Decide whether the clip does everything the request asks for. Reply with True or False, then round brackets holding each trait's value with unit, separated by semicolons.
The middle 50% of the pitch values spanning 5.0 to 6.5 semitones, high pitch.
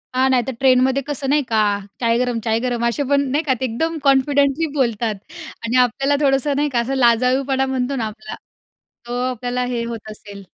False (2.7 semitones; 255 Hz)